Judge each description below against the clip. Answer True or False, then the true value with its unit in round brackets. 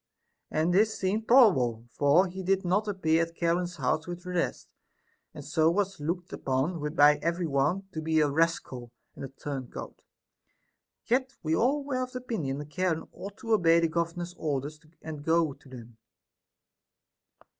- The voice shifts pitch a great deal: False (4.3 semitones)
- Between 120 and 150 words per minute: False (165 wpm)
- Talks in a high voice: False (165 Hz)